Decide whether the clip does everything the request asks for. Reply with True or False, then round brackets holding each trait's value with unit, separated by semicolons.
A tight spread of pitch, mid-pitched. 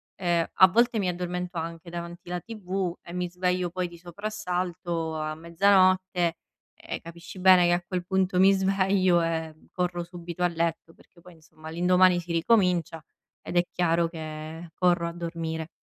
True (1.5 semitones; 175 Hz)